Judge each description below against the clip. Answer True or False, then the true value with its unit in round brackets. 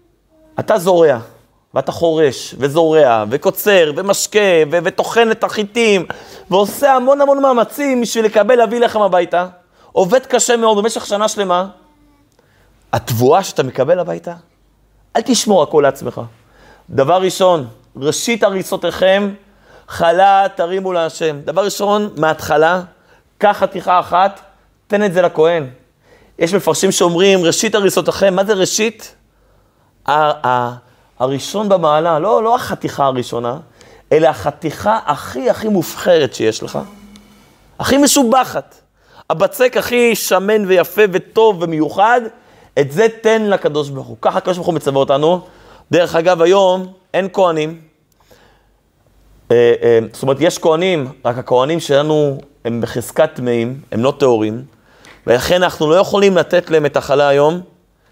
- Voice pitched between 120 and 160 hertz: False (180 Hz)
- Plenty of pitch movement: True (5.7 semitones)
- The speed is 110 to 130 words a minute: True (125 wpm)